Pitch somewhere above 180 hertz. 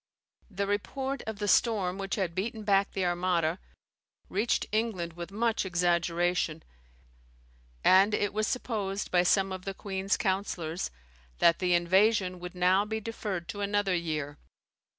Yes: high, 190 Hz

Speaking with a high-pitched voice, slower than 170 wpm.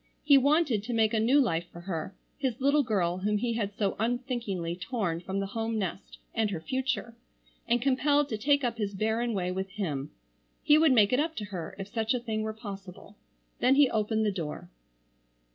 No: high, 220 Hz; fast, 205 wpm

